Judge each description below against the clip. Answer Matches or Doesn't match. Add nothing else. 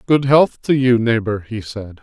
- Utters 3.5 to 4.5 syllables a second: Matches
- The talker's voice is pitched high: Doesn't match